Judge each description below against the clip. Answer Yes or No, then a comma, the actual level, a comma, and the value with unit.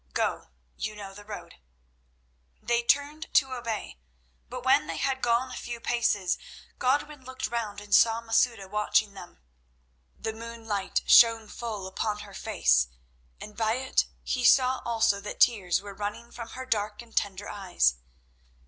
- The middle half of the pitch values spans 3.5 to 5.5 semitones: No, average, 2.7 semitones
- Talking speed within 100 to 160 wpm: Yes, average, 155 wpm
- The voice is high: Yes, high, 225 Hz